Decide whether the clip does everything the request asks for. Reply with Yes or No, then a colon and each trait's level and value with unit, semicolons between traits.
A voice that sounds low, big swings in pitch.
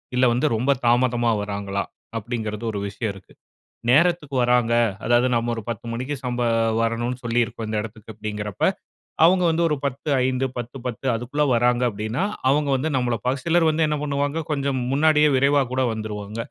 No: low, 125 Hz; average, 3.8 semitones